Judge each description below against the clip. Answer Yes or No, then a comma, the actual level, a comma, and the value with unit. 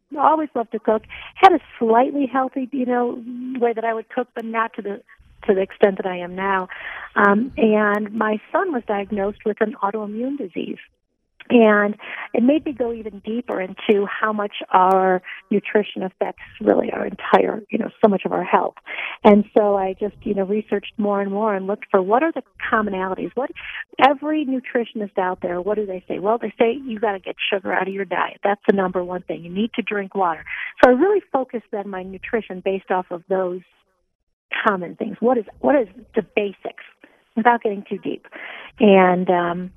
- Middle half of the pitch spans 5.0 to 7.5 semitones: No, average, 3.5 semitones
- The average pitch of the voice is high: Yes, high, 215 Hz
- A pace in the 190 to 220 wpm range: Yes, average, 200 wpm